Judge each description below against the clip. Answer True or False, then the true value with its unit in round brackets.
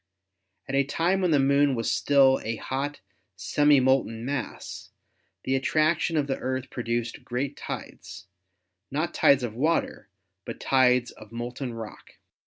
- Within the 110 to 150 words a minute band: True (145 wpm)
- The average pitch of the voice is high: False (135 Hz)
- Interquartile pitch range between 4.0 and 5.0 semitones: False (2.8 semitones)